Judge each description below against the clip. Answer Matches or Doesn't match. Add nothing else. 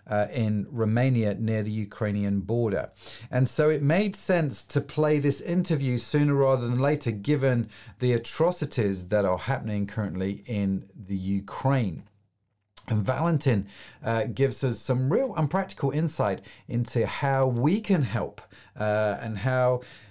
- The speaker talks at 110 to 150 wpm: Matches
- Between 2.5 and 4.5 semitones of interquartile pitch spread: Doesn't match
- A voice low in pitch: Matches